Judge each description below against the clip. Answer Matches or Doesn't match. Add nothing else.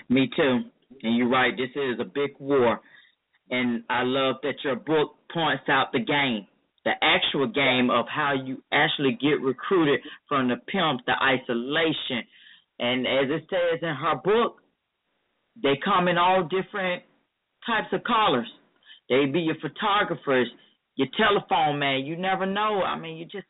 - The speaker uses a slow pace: Doesn't match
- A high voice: Doesn't match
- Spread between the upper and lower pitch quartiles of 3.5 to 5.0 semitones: Doesn't match